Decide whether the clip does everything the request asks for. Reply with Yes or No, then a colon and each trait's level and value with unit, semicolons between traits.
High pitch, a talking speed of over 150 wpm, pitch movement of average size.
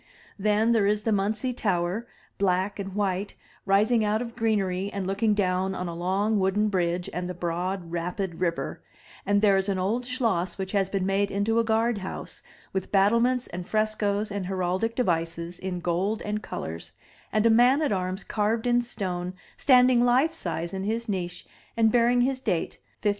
Yes: high, 200 Hz; average, 180 wpm; average, 3.4 semitones